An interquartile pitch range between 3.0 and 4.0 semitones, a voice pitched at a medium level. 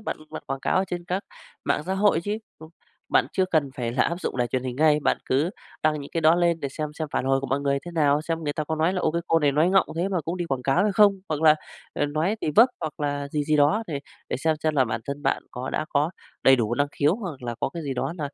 Yes: average, 3.4 semitones; medium, 155 Hz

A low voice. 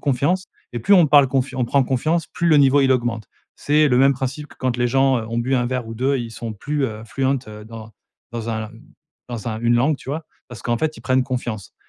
Yes: low, 130 Hz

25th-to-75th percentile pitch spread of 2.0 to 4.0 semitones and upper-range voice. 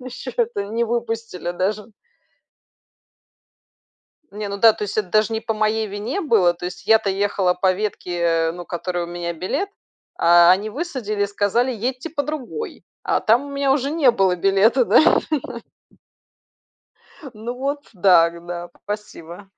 No: average, 5.0 semitones; high, 210 Hz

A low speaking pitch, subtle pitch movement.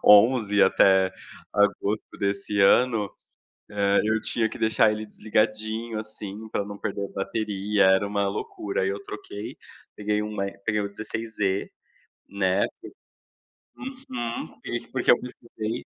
Yes: low, 105 Hz; narrow, 1.7 semitones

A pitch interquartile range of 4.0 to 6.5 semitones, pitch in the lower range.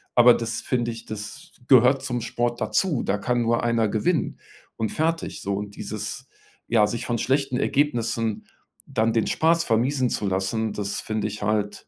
No: average, 2.8 semitones; low, 115 Hz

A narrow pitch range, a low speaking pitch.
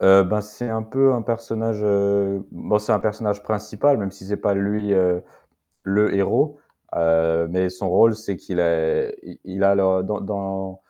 Yes: narrow, 2.1 semitones; low, 100 Hz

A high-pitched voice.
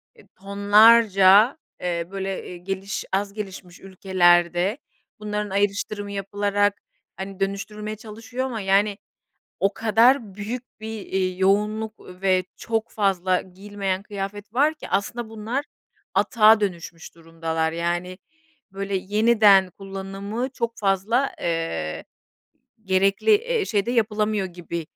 Yes: high, 200 Hz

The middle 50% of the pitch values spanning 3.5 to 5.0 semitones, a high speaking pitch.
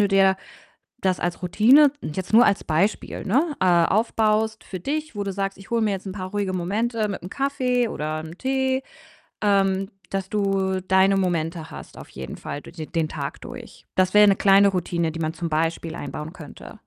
Yes: average, 3.8 semitones; high, 195 Hz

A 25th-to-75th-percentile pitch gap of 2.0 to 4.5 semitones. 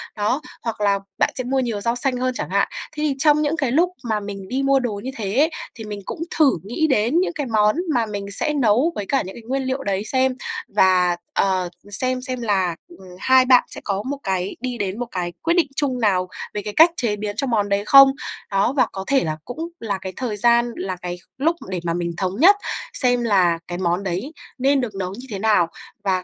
No: average, 5.1 semitones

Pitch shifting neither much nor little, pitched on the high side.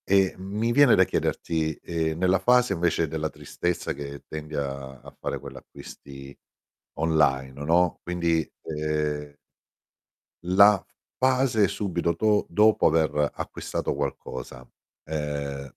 No: average, 4.5 semitones; very low, 80 Hz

